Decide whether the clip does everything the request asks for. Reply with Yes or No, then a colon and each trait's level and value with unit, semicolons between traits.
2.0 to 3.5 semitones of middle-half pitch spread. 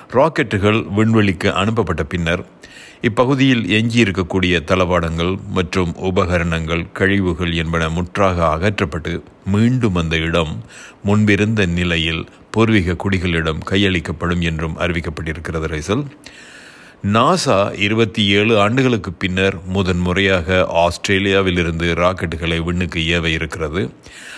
Yes: average, 3.1 semitones